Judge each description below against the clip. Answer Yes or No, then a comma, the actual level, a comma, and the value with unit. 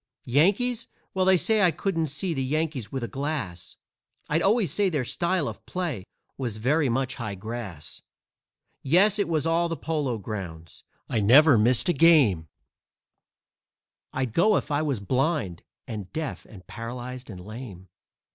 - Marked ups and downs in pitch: Yes, wide, 6.9 semitones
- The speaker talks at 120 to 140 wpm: No, average, 155 wpm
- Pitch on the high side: No, low, 135 Hz